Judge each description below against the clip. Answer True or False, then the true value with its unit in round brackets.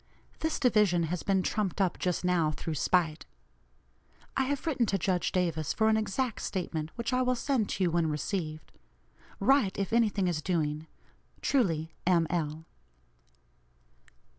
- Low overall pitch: False (185 Hz)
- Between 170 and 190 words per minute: False (155 wpm)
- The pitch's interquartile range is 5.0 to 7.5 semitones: True (5.3 semitones)